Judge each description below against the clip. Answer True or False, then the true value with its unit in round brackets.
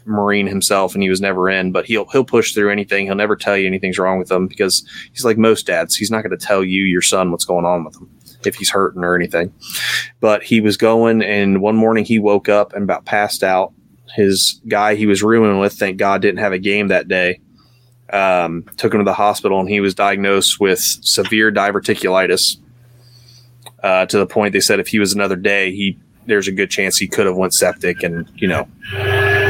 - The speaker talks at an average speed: False (220 wpm)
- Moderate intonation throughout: False (2.3 semitones)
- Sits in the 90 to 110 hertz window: True (100 Hz)